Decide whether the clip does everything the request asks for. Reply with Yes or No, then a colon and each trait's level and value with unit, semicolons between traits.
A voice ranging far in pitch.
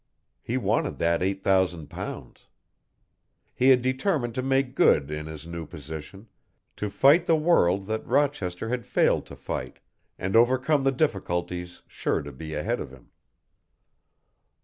Yes: wide, 7.5 semitones